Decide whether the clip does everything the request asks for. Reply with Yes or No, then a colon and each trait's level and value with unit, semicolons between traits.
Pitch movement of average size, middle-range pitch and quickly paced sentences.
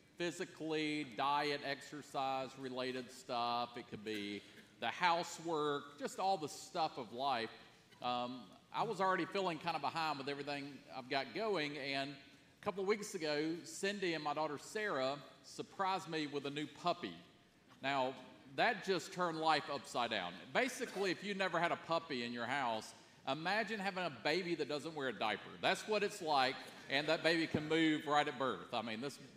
No: average, 4.3 semitones; medium, 150 Hz; average, 180 wpm